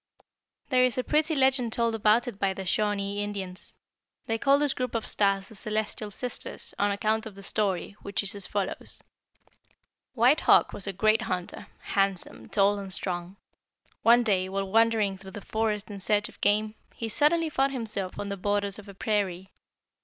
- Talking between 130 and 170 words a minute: No, average, 185 wpm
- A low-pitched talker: No, high, 205 Hz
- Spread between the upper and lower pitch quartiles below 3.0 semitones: Yes, narrow, 2.5 semitones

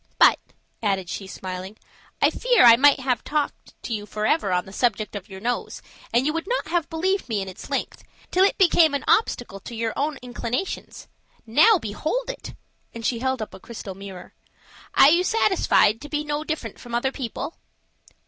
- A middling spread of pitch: No, wide, 6.7 semitones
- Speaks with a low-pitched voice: No, high, 245 Hz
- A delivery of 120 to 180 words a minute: No, average, 190 wpm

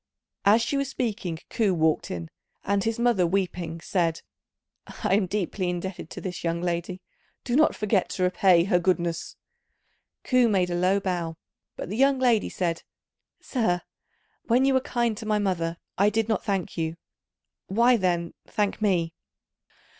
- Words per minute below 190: Yes, average, 160 wpm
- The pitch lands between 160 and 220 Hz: Yes, high, 190 Hz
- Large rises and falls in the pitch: No, average, 4.3 semitones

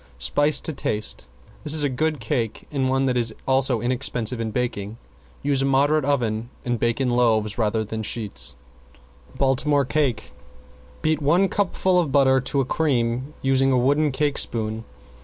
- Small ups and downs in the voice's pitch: No, average, 3.8 semitones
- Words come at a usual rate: Yes, average, 165 wpm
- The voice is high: No, low, 130 Hz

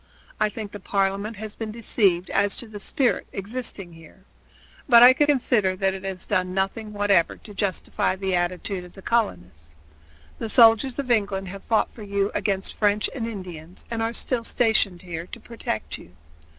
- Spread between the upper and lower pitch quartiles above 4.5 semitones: No, average, 3.3 semitones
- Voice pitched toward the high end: Yes, high, 200 Hz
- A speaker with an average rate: Yes, average, 175 wpm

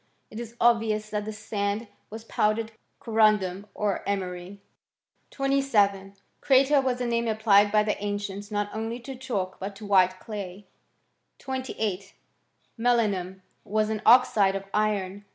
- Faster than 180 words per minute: No, slow, 135 wpm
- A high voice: Yes, high, 210 Hz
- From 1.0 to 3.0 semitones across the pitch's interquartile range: Yes, narrow, 2.4 semitones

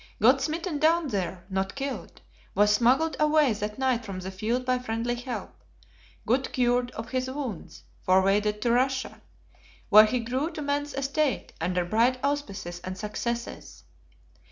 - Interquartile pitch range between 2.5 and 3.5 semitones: No, average, 4.6 semitones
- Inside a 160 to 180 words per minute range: No, average, 150 wpm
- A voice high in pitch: Yes, high, 245 Hz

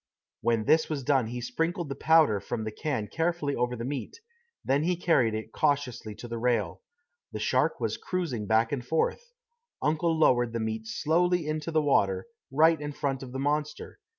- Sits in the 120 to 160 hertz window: Yes, medium, 140 Hz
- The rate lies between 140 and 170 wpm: No, average, 185 wpm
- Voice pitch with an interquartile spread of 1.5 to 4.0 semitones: No, average, 5.3 semitones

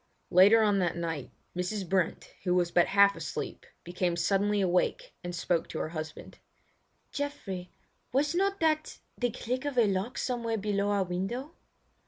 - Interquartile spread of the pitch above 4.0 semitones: Yes, wide, 5.5 semitones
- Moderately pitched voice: No, high, 200 Hz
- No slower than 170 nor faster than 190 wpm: No, average, 160 wpm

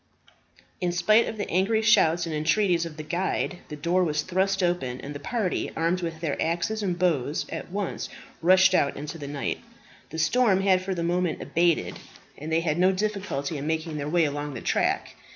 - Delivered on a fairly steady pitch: No, average, 3.4 semitones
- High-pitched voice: No, medium, 170 Hz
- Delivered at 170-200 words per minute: Yes, average, 195 wpm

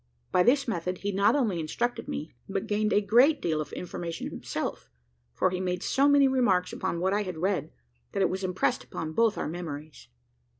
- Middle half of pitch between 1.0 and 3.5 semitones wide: No, average, 4.4 semitones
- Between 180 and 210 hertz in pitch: Yes, high, 190 Hz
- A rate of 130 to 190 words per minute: No, average, 200 wpm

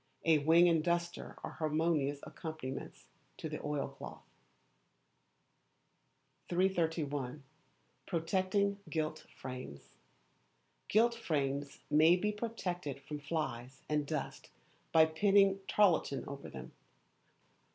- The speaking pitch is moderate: Yes, medium, 160 Hz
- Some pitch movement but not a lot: Yes, average, 3.9 semitones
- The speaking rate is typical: No, slow, 95 wpm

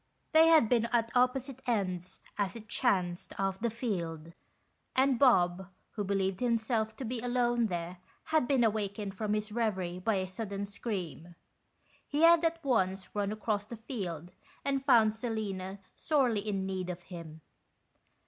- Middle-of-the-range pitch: No, high, 215 Hz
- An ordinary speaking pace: Yes, average, 155 wpm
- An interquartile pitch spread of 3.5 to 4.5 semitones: Yes, average, 4.2 semitones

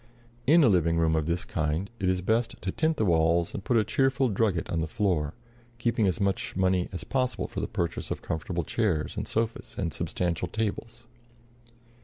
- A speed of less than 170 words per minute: No, average, 195 wpm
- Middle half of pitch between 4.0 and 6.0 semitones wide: Yes, average, 5.3 semitones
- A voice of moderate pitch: No, very low, 95 Hz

